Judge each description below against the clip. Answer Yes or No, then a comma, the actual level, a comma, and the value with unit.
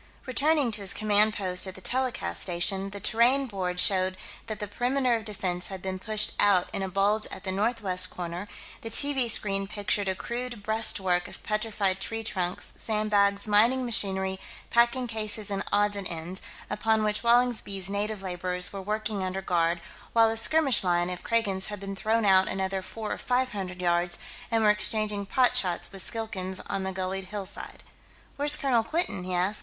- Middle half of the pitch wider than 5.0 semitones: No, average, 3.0 semitones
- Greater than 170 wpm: Yes, average, 185 wpm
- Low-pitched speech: No, high, 205 Hz